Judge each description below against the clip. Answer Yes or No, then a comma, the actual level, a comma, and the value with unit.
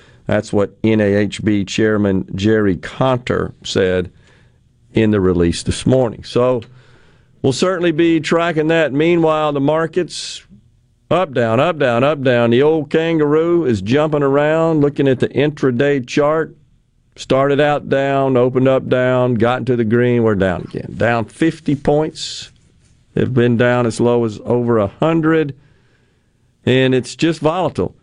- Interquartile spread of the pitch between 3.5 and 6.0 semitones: Yes, average, 4.4 semitones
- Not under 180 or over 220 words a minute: No, average, 140 wpm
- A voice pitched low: Yes, low, 125 Hz